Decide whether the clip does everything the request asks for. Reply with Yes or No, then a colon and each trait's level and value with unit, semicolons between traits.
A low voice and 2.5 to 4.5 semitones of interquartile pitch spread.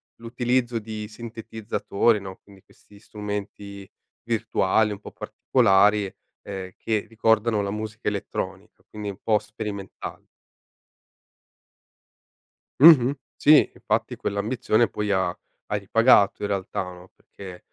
No: low, 105 Hz; narrow, 2.1 semitones